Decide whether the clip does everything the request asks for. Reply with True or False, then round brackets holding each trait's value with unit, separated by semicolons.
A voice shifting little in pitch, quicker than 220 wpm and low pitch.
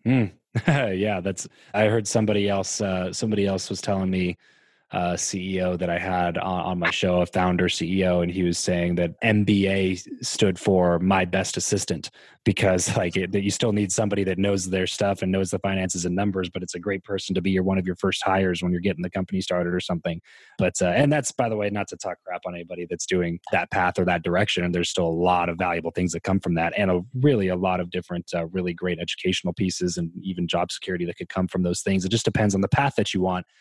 True (2.0 semitones; 245 wpm; 95 Hz)